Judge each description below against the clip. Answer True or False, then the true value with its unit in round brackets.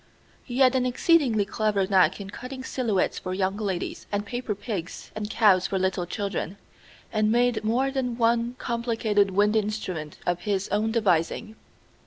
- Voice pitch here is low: False (215 Hz)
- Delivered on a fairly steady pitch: False (3.6 semitones)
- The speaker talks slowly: False (160 wpm)